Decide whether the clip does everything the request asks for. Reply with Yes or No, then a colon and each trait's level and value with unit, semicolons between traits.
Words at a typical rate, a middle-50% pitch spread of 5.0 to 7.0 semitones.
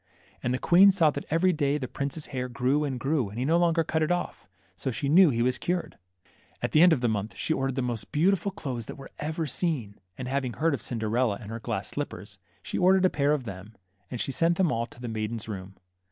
No: fast, 250 wpm; wide, 5.5 semitones